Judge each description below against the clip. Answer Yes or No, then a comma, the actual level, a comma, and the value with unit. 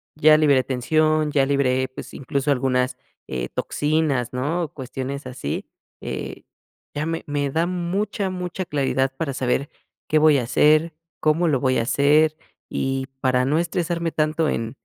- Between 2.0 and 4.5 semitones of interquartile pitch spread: Yes, average, 3.2 semitones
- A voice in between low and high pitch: Yes, medium, 145 Hz